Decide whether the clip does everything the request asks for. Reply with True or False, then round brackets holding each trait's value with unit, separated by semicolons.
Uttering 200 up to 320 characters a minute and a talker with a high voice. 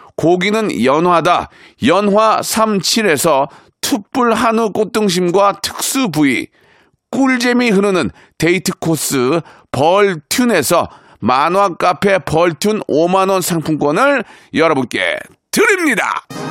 True (205 characters per minute; 205 Hz)